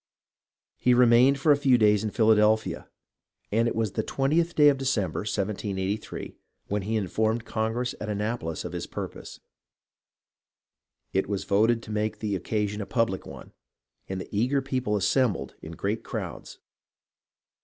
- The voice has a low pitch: Yes, low, 110 Hz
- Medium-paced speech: Yes, average, 155 wpm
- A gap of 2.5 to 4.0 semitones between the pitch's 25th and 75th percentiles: Yes, average, 3.0 semitones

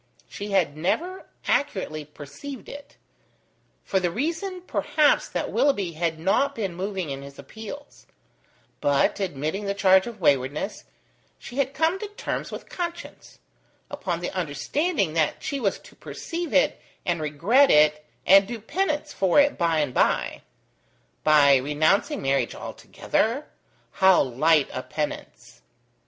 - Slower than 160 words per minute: Yes, average, 140 wpm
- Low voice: No, high, 190 Hz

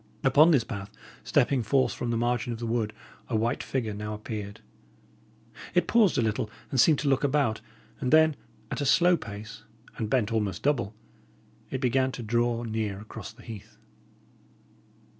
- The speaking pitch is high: No, low, 120 Hz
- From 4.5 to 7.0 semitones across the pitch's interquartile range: No, average, 3.7 semitones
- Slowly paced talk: No, average, 170 wpm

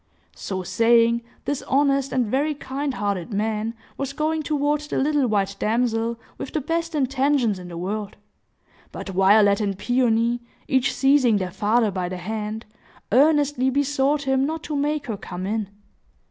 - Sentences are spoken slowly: No, average, 160 wpm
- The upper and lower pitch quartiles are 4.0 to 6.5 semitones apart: Yes, average, 5.1 semitones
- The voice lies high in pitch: Yes, high, 245 Hz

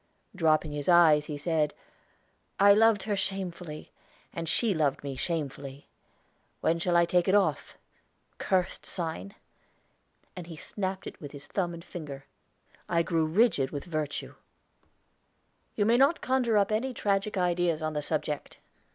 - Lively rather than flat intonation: No, average, 4.4 semitones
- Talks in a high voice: No, medium, 170 Hz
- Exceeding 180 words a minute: No, average, 150 wpm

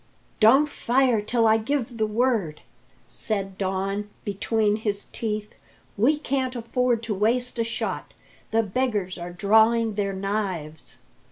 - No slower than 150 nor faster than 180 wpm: No, slow, 135 wpm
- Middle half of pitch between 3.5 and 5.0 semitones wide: No, average, 3.0 semitones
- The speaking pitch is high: Yes, high, 220 Hz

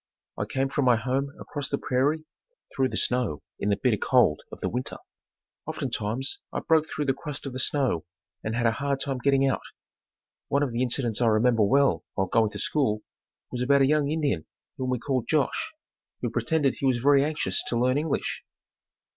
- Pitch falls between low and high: No, low, 130 Hz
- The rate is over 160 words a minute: Yes, average, 195 wpm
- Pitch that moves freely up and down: No, average, 2.9 semitones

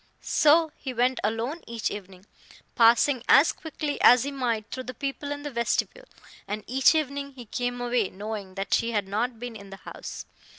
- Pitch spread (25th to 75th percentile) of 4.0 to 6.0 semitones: Yes, average, 4.4 semitones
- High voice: Yes, high, 245 Hz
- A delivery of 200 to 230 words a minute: No, average, 185 wpm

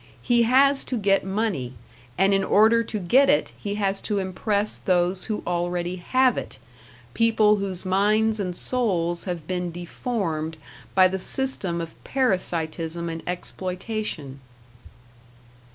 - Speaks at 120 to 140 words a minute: Yes, slow, 135 wpm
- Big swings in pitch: No, average, 3.9 semitones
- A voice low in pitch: No, high, 195 Hz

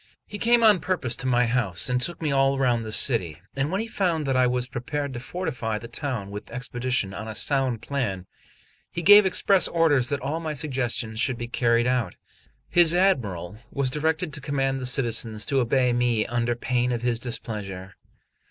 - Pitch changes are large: No, average, 3.9 semitones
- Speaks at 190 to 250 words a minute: Yes, average, 195 wpm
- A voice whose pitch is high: No, low, 125 Hz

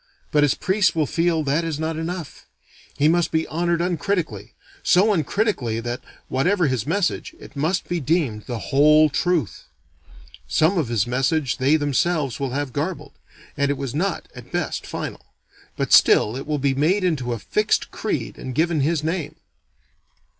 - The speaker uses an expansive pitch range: No, average, 4.2 semitones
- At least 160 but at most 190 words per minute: Yes, average, 170 wpm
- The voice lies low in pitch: No, medium, 155 Hz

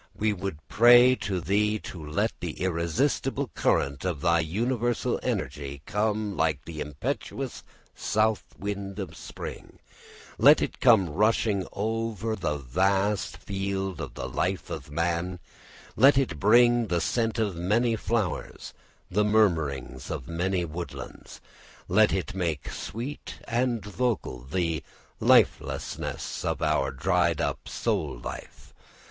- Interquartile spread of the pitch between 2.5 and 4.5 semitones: No, average, 4.9 semitones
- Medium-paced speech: No, slow, 130 wpm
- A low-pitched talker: Yes, very low, 95 Hz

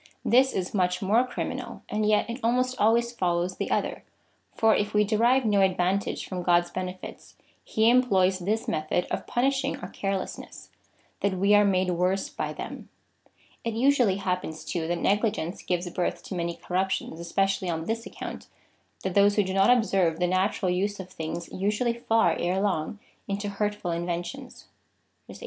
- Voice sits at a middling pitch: No, high, 195 Hz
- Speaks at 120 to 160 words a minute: No, average, 175 wpm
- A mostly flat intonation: No, average, 3.5 semitones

